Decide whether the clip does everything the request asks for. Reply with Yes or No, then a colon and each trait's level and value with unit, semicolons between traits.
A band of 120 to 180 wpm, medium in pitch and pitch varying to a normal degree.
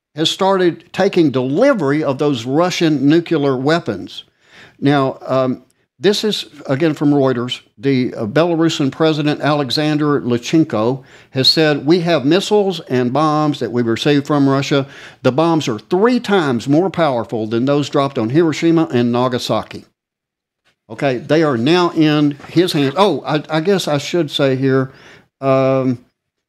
Yes: average, 145 wpm; medium, 145 Hz; average, 3.8 semitones